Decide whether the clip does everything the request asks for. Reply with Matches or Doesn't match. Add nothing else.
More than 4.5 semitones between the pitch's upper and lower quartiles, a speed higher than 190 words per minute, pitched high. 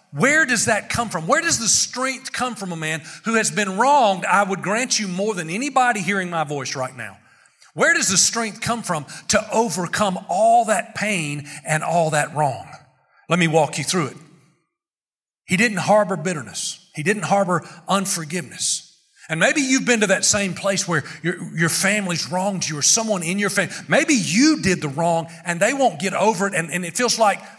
Matches